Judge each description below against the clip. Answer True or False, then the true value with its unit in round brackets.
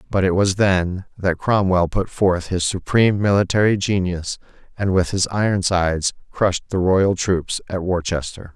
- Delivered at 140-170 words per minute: True (155 wpm)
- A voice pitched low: True (95 Hz)